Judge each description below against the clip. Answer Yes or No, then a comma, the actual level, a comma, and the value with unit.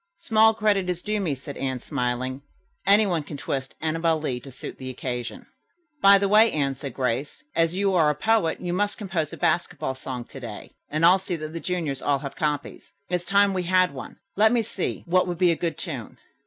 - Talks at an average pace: No, fast, 215 wpm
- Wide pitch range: Yes, wide, 5.8 semitones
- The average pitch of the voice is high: No, medium, 165 Hz